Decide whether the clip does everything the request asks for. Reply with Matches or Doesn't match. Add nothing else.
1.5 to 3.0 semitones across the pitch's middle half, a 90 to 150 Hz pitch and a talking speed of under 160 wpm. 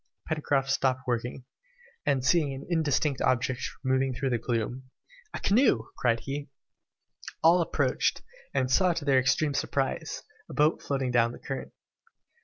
Matches